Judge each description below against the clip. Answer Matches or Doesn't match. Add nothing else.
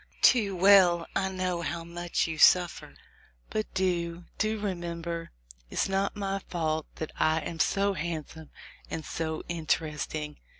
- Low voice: Doesn't match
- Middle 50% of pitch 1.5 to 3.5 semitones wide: Matches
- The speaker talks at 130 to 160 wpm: Matches